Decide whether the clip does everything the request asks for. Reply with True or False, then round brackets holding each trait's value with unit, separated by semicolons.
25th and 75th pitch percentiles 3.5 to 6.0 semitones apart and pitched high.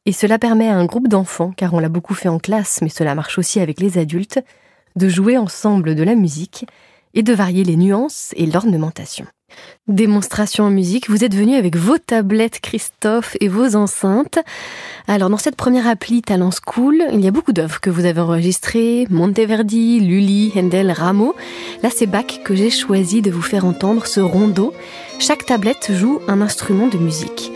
True (3.9 semitones; 205 Hz)